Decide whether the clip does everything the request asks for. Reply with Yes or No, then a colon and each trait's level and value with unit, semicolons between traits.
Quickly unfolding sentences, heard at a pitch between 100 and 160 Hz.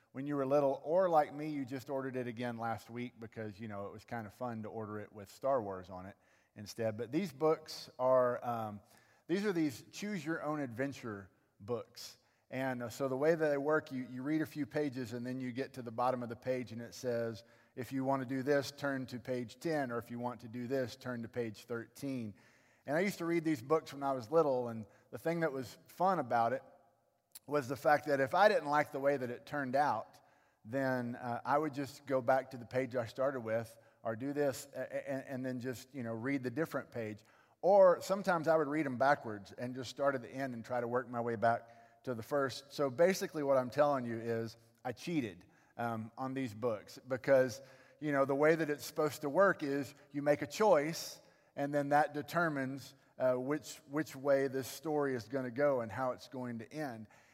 Yes: fast, 230 wpm; low, 130 Hz